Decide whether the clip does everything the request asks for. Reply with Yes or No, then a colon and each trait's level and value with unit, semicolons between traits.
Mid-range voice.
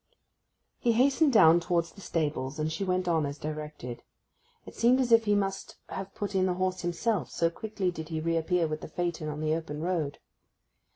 Yes: medium, 170 Hz